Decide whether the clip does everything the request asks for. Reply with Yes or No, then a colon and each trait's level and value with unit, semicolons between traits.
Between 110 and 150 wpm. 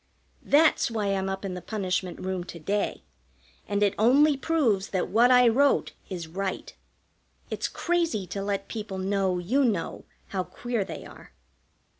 No: average, 160 wpm